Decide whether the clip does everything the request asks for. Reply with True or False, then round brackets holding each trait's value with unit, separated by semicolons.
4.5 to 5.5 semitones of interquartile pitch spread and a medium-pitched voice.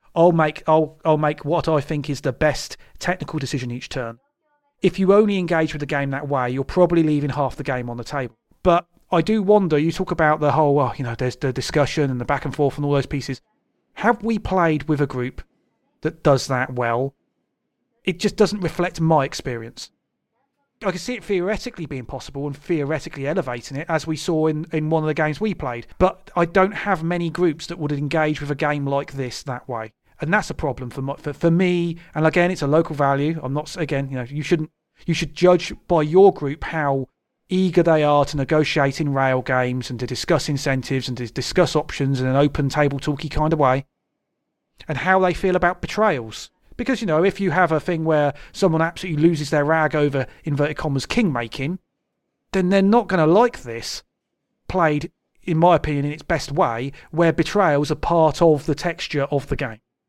False (3.8 semitones; 155 Hz)